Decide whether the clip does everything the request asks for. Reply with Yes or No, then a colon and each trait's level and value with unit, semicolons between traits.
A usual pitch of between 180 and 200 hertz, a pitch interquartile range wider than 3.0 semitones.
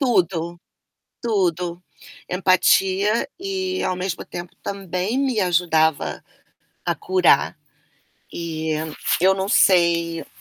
Yes: medium, 185 Hz; average, 3.6 semitones